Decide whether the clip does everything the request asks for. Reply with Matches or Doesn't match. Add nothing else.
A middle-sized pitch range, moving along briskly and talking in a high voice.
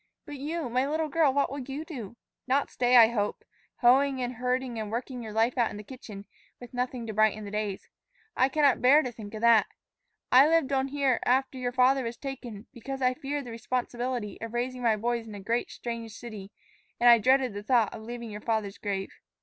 Matches